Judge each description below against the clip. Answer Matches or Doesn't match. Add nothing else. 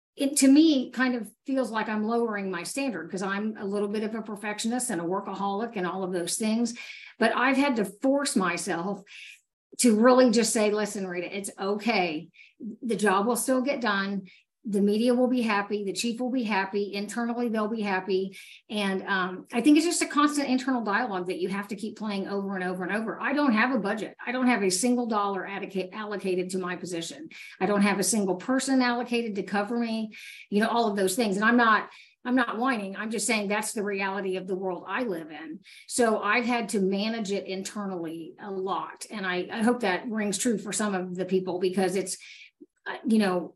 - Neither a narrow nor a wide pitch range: Matches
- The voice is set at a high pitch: Matches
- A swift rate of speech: Matches